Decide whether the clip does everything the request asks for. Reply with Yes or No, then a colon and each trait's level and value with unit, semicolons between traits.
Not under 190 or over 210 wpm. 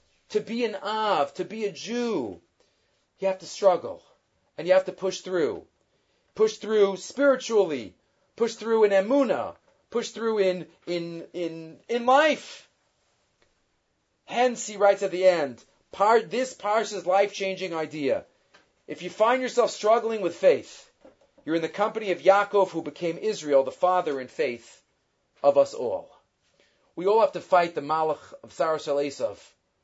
No: average, 155 wpm